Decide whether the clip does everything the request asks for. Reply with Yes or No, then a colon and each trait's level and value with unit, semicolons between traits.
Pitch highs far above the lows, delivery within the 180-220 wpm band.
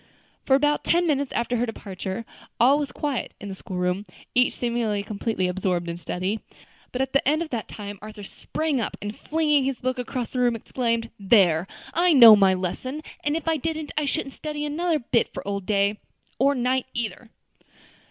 Yes: wide, 5.8 semitones; average, 190 wpm